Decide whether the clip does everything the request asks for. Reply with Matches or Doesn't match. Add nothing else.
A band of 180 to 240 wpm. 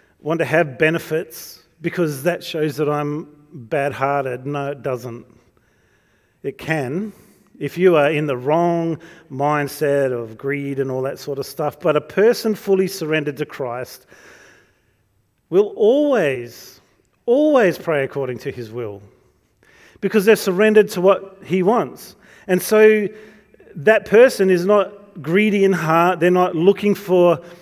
Doesn't match